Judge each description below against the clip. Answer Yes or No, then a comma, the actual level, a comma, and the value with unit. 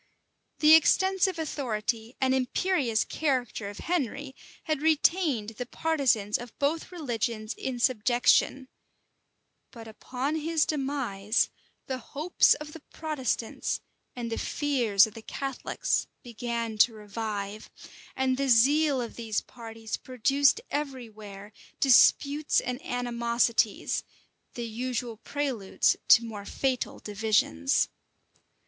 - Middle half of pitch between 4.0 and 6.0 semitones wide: Yes, average, 4.3 semitones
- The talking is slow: Yes, slow, 115 wpm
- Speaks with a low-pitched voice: No, high, 245 Hz